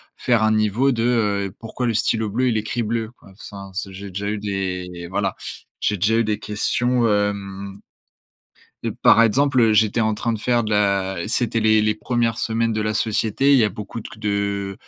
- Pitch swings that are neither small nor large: No, narrow, 2.3 semitones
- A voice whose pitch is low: Yes, low, 105 Hz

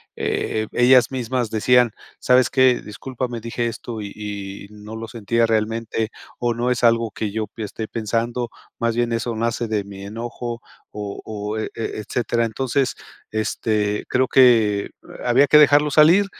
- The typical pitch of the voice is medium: No, low, 115 Hz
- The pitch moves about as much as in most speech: No, narrow, 2.3 semitones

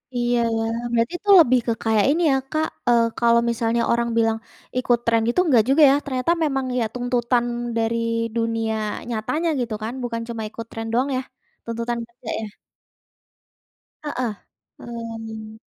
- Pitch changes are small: Yes, narrow, 1.8 semitones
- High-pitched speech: Yes, high, 235 Hz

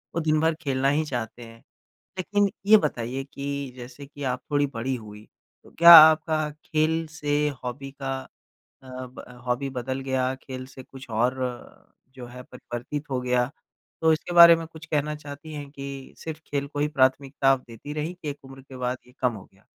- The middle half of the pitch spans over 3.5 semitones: No, average, 3.1 semitones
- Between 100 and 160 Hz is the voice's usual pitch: Yes, low, 135 Hz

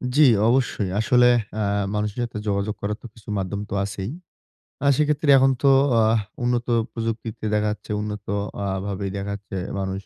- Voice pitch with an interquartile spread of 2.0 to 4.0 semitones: Yes, average, 3.1 semitones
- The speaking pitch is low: Yes, low, 105 Hz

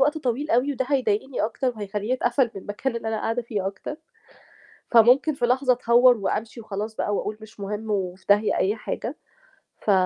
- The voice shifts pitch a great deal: No, average, 3.4 semitones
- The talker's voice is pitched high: Yes, high, 230 Hz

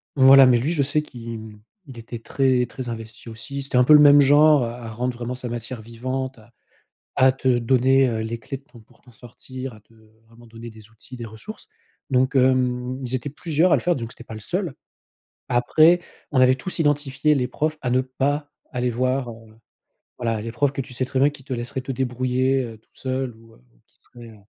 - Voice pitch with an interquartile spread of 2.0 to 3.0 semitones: Yes, narrow, 2.5 semitones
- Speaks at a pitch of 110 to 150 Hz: Yes, low, 125 Hz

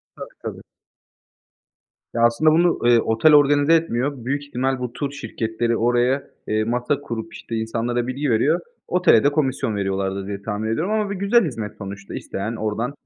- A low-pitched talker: Yes, low, 120 Hz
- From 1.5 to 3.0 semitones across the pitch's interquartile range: No, average, 4.4 semitones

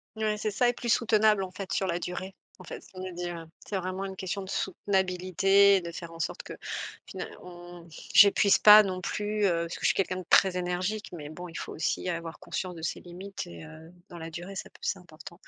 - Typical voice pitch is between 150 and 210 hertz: Yes, medium, 185 Hz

